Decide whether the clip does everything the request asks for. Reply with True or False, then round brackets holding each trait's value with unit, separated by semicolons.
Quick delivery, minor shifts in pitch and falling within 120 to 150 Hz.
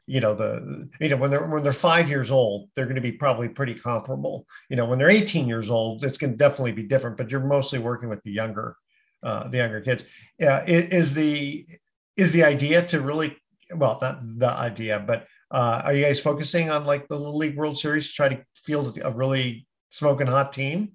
False (220 wpm; 3.6 semitones; 140 Hz)